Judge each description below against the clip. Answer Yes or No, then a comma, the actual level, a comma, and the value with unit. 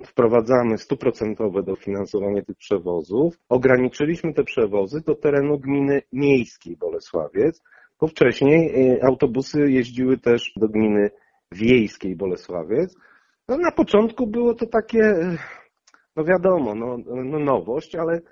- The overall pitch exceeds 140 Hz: No, low, 135 Hz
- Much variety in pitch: Yes, wide, 5.7 semitones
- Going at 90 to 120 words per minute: Yes, slow, 110 wpm